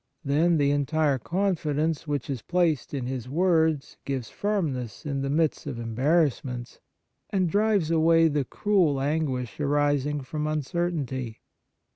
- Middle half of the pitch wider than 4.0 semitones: No, average, 3.4 semitones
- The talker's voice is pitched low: No, medium, 150 Hz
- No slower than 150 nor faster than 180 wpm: No, slow, 135 wpm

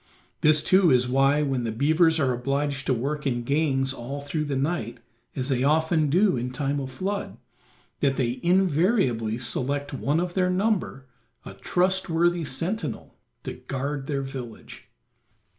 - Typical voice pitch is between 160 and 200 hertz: No, medium, 140 Hz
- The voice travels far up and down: No, average, 3.9 semitones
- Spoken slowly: No, average, 155 wpm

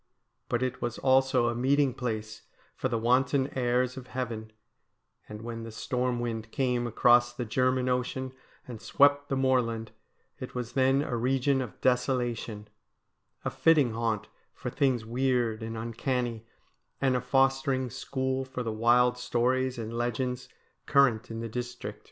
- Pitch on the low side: Yes, low, 125 Hz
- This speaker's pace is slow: No, average, 150 wpm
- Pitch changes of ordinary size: No, narrow, 2.0 semitones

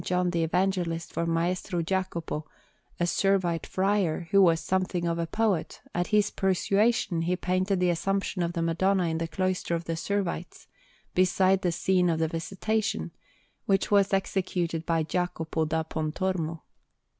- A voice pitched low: No, medium, 180 Hz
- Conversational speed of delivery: Yes, average, 155 wpm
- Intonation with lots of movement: No, narrow, 2.4 semitones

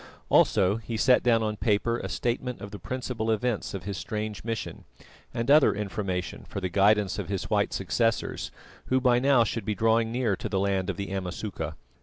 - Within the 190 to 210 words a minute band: Yes, average, 195 wpm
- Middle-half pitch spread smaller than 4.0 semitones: Yes, average, 3.0 semitones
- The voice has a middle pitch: No, low, 105 Hz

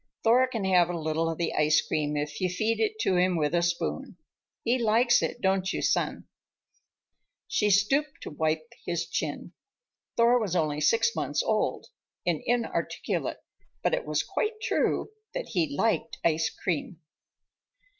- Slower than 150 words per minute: No, average, 160 wpm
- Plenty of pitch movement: Yes, wide, 6.7 semitones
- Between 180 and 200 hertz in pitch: Yes, medium, 185 Hz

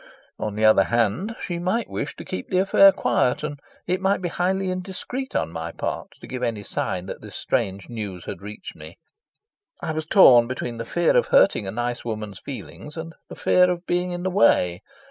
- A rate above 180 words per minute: Yes, fast, 205 wpm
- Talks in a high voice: No, medium, 145 Hz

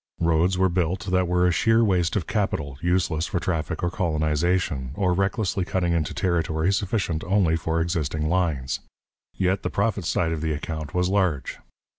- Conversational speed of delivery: Yes, average, 170 wpm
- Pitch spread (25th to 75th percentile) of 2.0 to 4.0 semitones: Yes, average, 2.8 semitones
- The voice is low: Yes, very low, 90 Hz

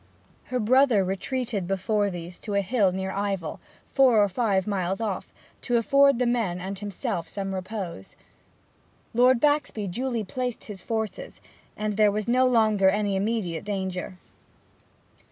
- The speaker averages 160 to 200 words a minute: No, average, 145 wpm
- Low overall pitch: No, high, 205 Hz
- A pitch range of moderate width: Yes, average, 3.8 semitones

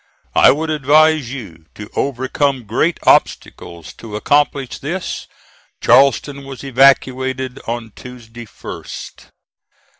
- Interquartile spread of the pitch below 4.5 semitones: Yes, average, 3.1 semitones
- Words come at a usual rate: No, slow, 100 wpm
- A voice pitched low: Yes, low, 130 Hz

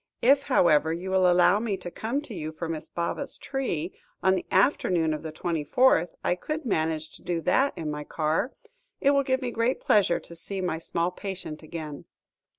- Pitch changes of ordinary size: No, wide, 6.2 semitones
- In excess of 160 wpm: Yes, average, 200 wpm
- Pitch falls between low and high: Yes, medium, 180 Hz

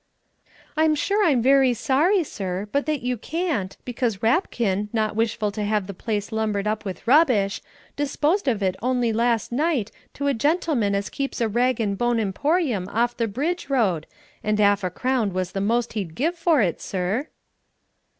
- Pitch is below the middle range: No, high, 230 Hz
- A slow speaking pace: No, average, 180 wpm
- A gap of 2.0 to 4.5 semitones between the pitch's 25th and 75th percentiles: No, wide, 5.4 semitones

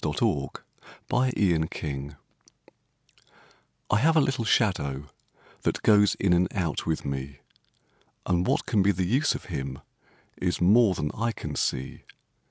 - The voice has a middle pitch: No, very low, 90 Hz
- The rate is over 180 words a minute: No, average, 145 wpm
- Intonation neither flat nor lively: No, wide, 7.0 semitones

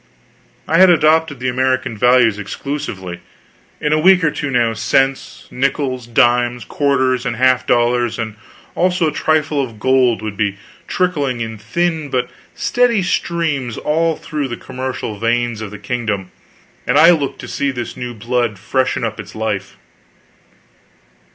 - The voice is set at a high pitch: No, low, 130 Hz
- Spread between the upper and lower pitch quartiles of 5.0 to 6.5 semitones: No, average, 4.4 semitones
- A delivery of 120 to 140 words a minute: No, average, 150 wpm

